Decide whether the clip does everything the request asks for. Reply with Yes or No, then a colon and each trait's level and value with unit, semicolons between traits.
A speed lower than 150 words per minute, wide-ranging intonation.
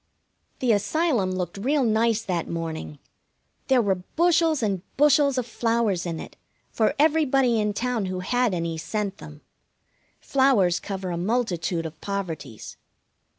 Yes: average, 140 wpm; wide, 5.9 semitones